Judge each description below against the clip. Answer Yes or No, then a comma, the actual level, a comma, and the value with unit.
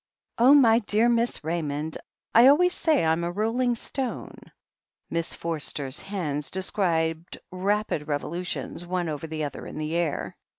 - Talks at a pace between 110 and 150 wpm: Yes, average, 140 wpm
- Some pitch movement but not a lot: No, wide, 6.1 semitones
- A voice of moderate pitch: Yes, medium, 175 Hz